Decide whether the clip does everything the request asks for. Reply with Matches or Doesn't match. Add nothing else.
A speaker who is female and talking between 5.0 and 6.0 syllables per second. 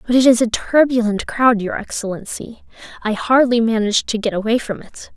Matches